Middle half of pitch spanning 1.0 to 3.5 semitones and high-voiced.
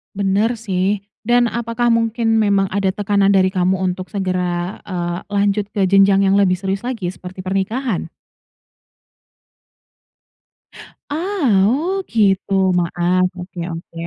Yes: average, 3.2 semitones; high, 195 Hz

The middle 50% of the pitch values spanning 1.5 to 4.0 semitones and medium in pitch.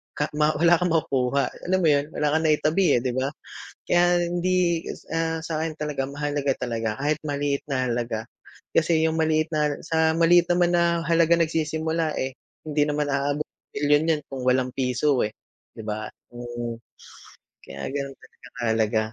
Yes: average, 3.7 semitones; medium, 150 Hz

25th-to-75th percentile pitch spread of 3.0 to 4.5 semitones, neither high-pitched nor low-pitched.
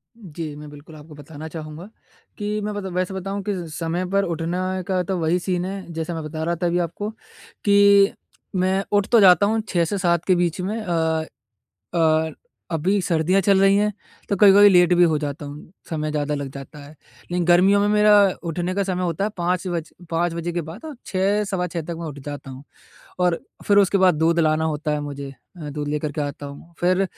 Yes: average, 3.5 semitones; medium, 175 Hz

